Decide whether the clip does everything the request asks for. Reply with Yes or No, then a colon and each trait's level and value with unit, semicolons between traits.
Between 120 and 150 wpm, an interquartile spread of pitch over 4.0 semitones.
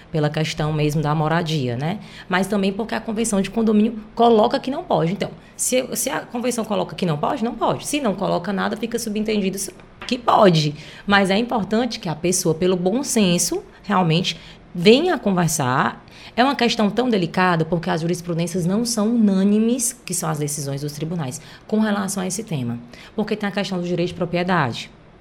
No: fast, 185 wpm; average, 4.6 semitones